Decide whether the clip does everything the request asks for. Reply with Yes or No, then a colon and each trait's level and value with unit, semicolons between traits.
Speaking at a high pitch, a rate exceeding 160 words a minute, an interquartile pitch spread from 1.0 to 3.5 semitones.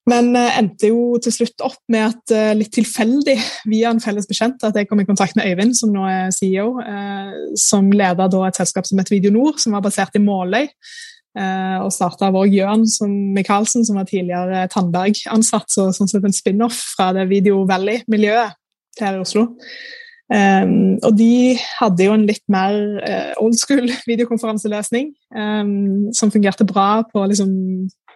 Yes: high, 210 Hz; average, 180 wpm; average, 2.9 semitones